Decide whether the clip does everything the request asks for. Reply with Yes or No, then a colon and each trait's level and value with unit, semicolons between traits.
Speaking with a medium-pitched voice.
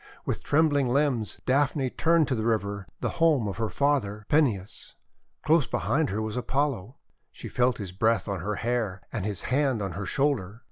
No: low, 120 Hz